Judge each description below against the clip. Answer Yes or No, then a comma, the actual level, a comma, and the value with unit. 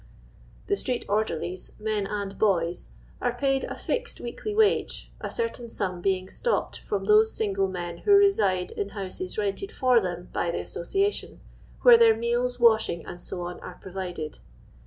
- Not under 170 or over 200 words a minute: No, average, 155 wpm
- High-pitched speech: Yes, high, 210 Hz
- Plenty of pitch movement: Yes, wide, 6.7 semitones